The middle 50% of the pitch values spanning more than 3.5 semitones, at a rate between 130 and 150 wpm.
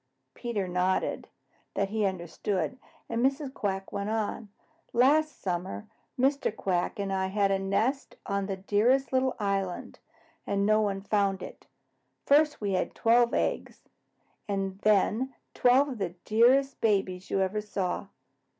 Yes: average, 4.0 semitones; average, 140 wpm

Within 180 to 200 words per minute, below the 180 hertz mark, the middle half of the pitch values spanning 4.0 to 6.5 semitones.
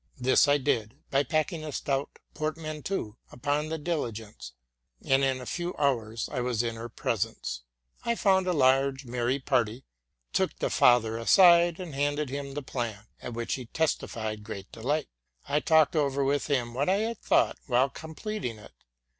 No: average, 170 wpm; low, 135 Hz; average, 4.6 semitones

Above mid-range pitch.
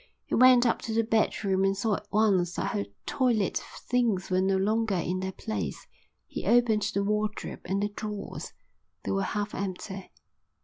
Yes: high, 205 Hz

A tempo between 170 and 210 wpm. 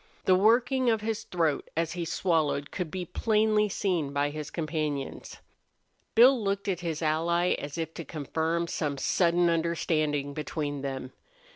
No: average, 150 wpm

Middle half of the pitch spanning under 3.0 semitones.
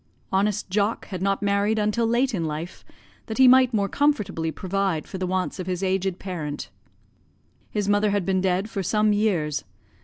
Yes: narrow, 2.4 semitones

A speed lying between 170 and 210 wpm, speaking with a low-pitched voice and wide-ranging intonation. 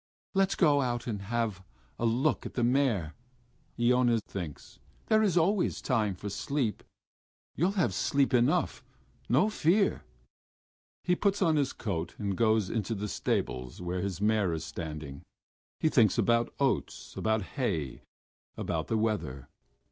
No: average, 145 wpm; low, 115 Hz; wide, 6.5 semitones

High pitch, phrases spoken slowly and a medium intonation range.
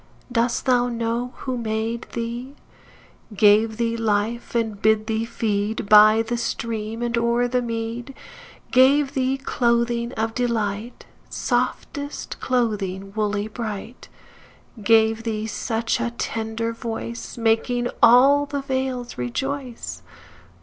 No: high, 230 Hz; slow, 115 wpm; narrow, 1.9 semitones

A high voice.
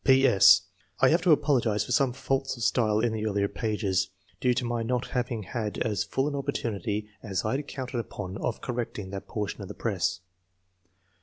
No: low, 115 Hz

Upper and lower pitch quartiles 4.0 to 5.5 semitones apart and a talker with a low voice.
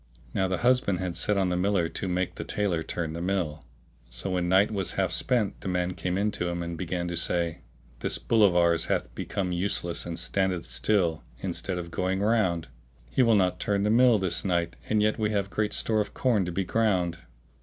No: average, 3.0 semitones; very low, 95 Hz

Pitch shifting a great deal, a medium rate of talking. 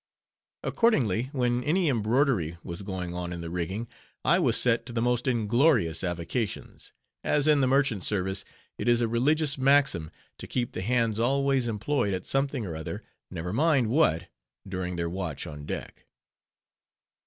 Yes: wide, 7.0 semitones; average, 160 wpm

